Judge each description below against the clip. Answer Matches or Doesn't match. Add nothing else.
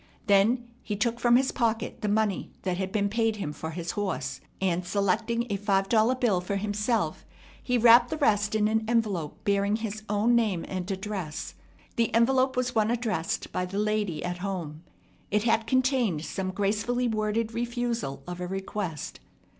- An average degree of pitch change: Matches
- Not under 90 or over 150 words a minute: Doesn't match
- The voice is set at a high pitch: Matches